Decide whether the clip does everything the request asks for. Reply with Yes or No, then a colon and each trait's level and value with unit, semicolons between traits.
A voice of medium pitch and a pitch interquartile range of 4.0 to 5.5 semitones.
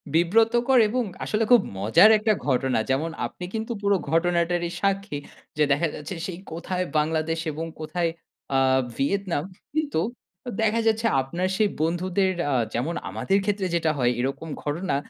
Yes: medium, 175 Hz; average, 4.6 semitones